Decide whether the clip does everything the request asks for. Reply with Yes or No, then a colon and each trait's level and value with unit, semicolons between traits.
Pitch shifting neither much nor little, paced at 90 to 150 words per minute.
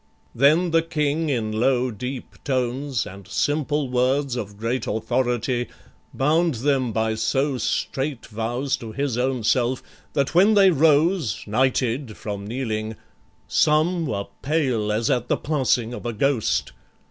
Yes: average, 4.2 semitones; average, 140 wpm